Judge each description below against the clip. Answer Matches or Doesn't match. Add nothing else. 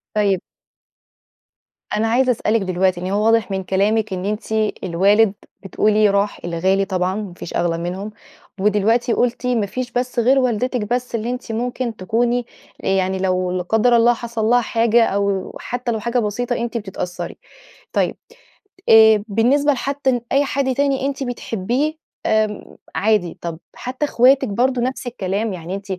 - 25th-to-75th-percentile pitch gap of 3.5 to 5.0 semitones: Matches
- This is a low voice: Doesn't match